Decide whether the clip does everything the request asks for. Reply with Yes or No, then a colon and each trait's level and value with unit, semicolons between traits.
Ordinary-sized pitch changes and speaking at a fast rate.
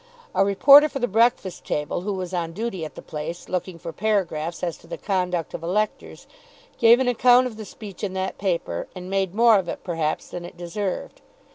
Yes: average, 4.0 semitones; fast, 210 wpm